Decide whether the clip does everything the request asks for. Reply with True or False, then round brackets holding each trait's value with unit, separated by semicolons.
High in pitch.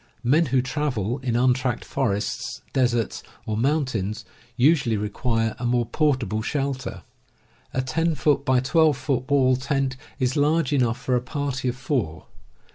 False (130 Hz)